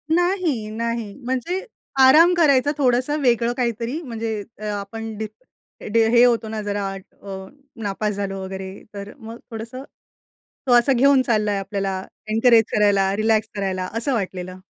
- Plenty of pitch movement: No, average, 3.7 semitones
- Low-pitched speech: No, high, 225 Hz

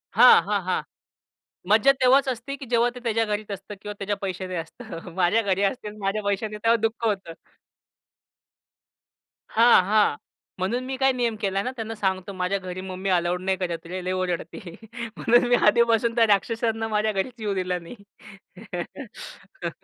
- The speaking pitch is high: Yes, high, 205 Hz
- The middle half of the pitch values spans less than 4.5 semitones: Yes, average, 3.5 semitones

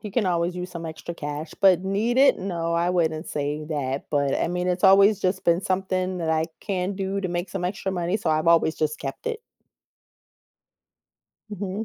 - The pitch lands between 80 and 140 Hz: No, medium, 180 Hz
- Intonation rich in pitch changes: No, average, 3.1 semitones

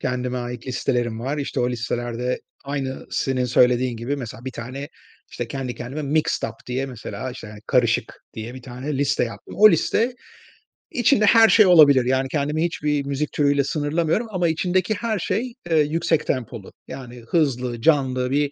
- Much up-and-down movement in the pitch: No, average, 3.7 semitones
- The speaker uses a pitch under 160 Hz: Yes, low, 135 Hz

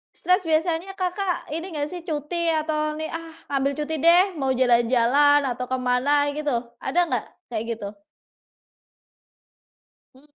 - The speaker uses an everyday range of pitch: Yes, average, 4.1 semitones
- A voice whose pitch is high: Yes, very high, 295 Hz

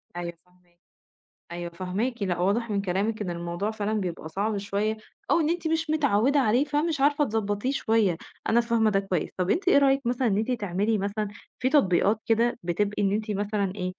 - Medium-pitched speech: No, high, 210 Hz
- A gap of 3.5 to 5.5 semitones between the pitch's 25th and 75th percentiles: Yes, average, 4.2 semitones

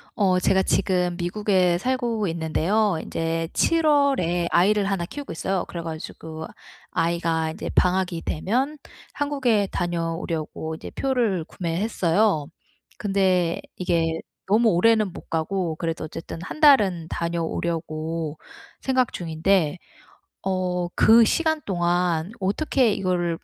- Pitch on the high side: No, medium, 180 Hz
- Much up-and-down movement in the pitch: No, average, 4.1 semitones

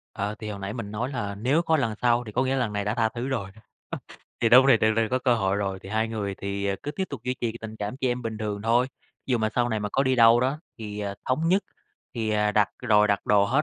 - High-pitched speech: No, low, 110 Hz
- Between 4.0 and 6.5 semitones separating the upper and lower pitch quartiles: No, average, 3.4 semitones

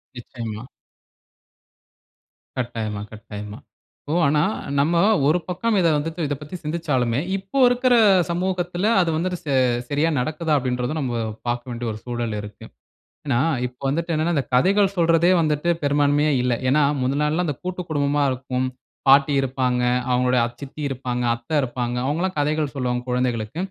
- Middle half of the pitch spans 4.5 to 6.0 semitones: Yes, average, 5.0 semitones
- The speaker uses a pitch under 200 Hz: Yes, medium, 140 Hz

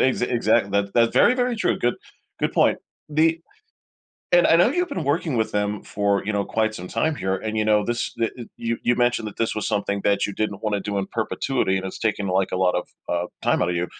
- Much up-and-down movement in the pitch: No, average, 3.5 semitones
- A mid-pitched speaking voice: No, low, 110 Hz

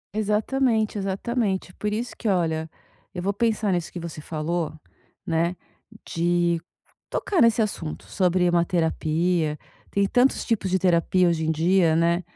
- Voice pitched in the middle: Yes, medium, 180 Hz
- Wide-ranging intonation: No, average, 3.8 semitones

